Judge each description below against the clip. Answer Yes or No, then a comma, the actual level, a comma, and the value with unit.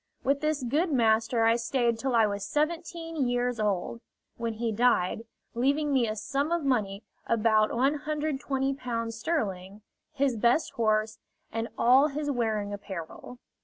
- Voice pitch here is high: Yes, high, 240 Hz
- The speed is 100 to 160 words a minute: Yes, average, 140 wpm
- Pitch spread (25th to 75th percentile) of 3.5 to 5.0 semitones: Yes, average, 4.3 semitones